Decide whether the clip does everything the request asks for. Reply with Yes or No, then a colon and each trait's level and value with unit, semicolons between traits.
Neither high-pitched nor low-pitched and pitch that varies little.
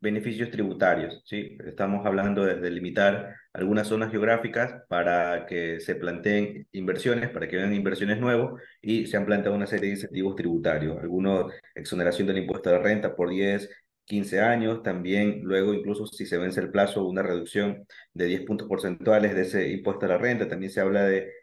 No: low, 100 Hz; narrow, 2.0 semitones